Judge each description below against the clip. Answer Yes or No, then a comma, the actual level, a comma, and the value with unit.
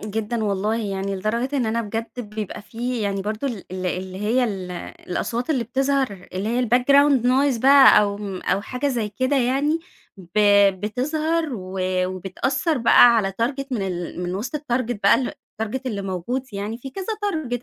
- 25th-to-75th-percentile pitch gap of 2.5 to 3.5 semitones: No, average, 4.7 semitones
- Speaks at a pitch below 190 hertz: No, high, 230 Hz